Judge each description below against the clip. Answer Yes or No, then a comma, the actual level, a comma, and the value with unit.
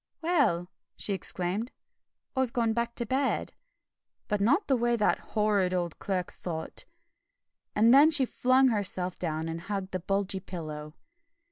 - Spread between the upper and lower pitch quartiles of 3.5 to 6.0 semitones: Yes, average, 5.0 semitones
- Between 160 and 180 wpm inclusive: No, average, 145 wpm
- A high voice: Yes, high, 205 Hz